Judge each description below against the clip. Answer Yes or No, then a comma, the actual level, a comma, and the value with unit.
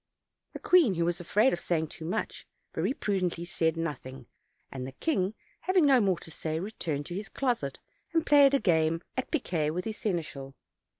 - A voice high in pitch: No, medium, 175 Hz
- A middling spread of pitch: No, wide, 6.2 semitones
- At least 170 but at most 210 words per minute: Yes, average, 190 wpm